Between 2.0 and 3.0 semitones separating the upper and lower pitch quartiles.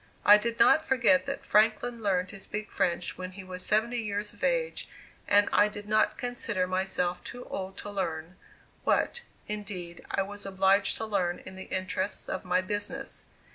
Yes: narrow, 2.5 semitones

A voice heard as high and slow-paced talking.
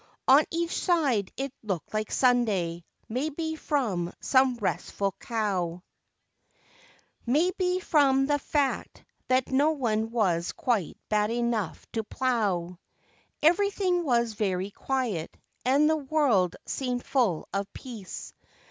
Yes: high, 245 Hz; slow, 120 wpm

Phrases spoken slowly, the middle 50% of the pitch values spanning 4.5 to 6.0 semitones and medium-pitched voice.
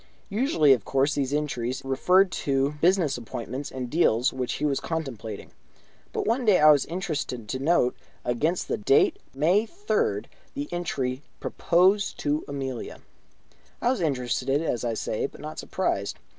No: average, 155 wpm; wide, 5.6 semitones; medium, 145 Hz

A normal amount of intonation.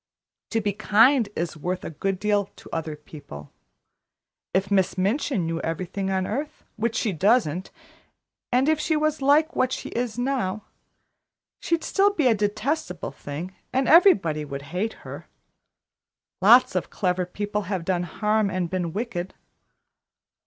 No: wide, 5.7 semitones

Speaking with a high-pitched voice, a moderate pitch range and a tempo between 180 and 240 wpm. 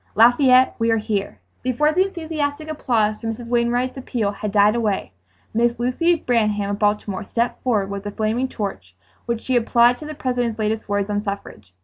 Yes: high, 230 Hz; average, 3.4 semitones; average, 185 wpm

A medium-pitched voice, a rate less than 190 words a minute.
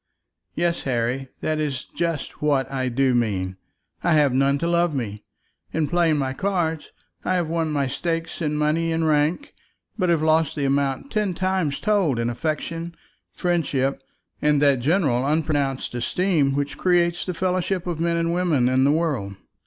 Yes: medium, 155 Hz; average, 170 wpm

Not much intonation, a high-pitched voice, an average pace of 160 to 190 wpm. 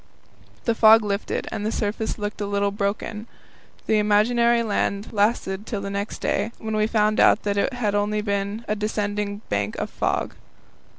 Yes: narrow, 1.4 semitones; high, 210 Hz; average, 175 wpm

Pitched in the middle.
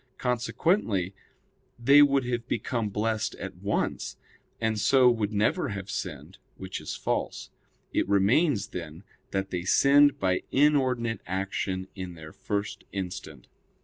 No: low, 105 Hz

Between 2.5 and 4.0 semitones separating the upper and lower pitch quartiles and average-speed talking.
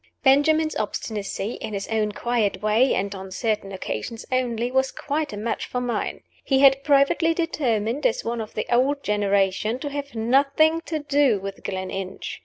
No: average, 5.1 semitones; average, 170 wpm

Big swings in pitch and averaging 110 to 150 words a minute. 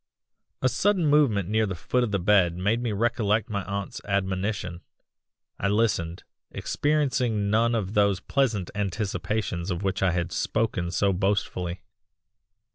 No: average, 3.4 semitones; average, 140 wpm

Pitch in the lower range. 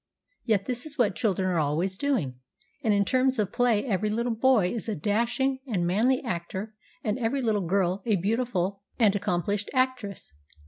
No: high, 210 Hz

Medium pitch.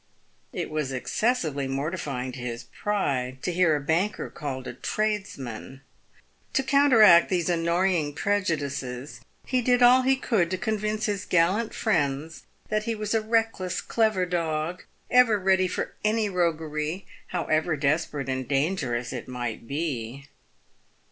Yes: medium, 170 Hz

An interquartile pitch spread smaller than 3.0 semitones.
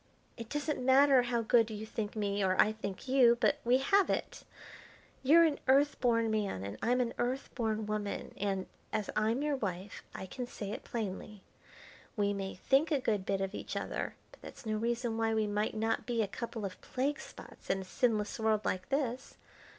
No: average, 3.6 semitones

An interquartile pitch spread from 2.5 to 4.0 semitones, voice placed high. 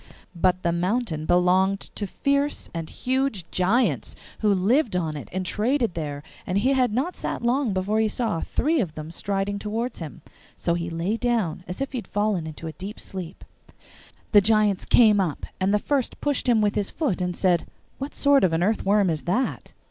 No: average, 5.1 semitones; high, 200 Hz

